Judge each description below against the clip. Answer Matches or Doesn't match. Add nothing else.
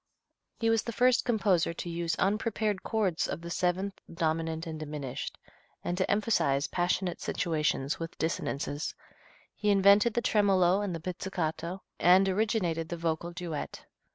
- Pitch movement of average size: Matches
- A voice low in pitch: Doesn't match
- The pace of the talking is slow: Doesn't match